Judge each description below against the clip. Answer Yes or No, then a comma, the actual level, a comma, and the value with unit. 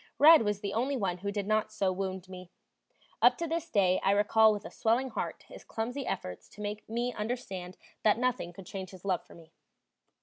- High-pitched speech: Yes, high, 205 Hz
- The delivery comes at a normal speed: No, fast, 210 wpm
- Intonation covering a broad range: No, average, 3.8 semitones